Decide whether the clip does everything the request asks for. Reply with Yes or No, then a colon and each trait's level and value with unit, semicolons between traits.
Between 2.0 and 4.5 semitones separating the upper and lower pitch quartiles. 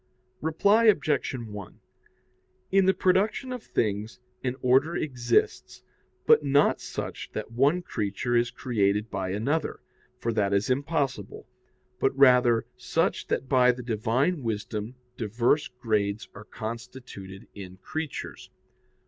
No: average, 4.9 semitones